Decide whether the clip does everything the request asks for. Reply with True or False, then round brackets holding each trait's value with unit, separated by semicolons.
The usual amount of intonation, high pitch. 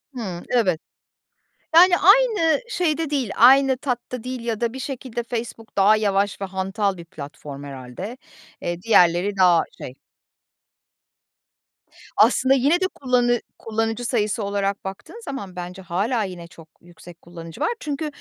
False (6.1 semitones; 220 Hz)